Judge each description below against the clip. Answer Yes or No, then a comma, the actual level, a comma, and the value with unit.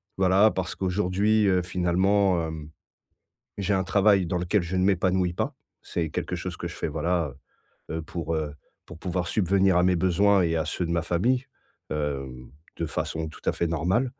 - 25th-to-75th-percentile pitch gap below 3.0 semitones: Yes, narrow, 2.6 semitones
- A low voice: Yes, very low, 90 Hz